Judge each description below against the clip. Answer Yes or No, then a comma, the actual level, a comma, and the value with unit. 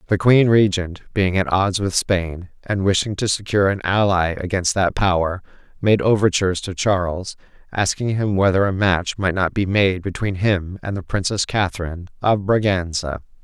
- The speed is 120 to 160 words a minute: No, average, 170 wpm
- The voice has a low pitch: Yes, very low, 95 Hz